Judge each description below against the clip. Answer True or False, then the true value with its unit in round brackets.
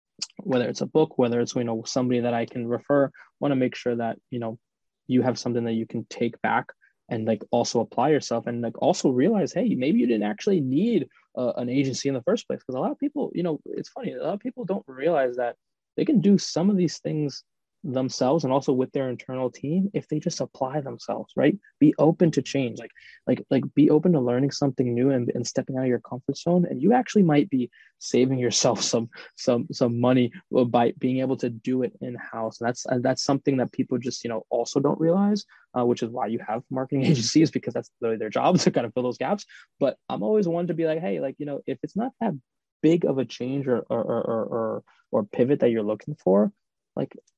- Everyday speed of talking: False (235 wpm)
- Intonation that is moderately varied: True (4.0 semitones)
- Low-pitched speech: True (130 Hz)